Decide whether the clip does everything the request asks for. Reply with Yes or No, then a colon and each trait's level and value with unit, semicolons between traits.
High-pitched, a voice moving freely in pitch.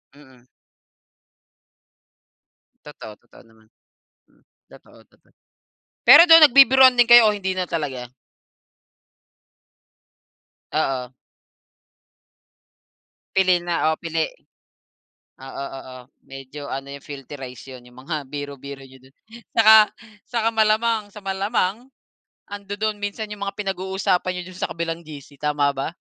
No: medium, 165 Hz; wide, 6.9 semitones